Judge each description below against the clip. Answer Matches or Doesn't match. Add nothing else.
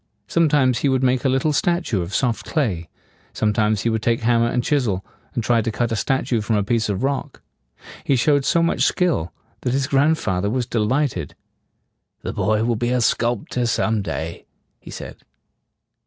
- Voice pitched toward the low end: Matches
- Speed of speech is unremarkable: Matches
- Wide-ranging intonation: Doesn't match